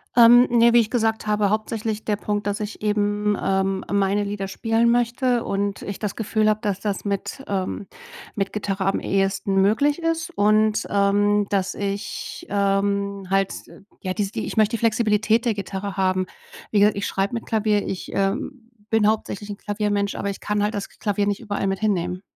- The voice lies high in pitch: Yes, high, 205 Hz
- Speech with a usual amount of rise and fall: No, narrow, 1.7 semitones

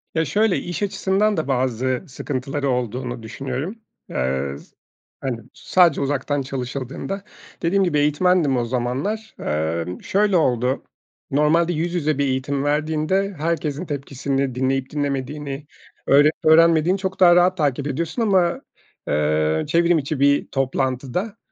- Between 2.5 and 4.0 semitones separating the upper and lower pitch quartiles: No, average, 4.7 semitones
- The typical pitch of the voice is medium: Yes, medium, 145 Hz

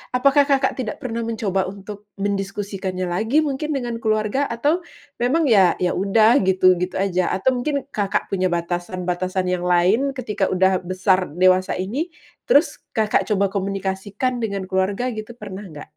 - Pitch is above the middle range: Yes, high, 200 Hz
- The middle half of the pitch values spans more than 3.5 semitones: Yes, average, 3.9 semitones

